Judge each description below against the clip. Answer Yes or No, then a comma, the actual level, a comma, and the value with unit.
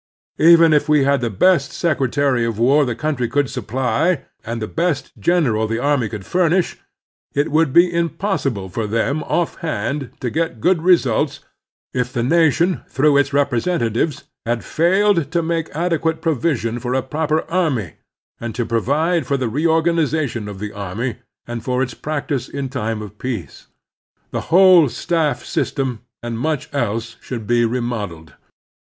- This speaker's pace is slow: No, average, 160 wpm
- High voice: No, medium, 140 Hz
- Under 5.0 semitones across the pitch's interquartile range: No, wide, 5.6 semitones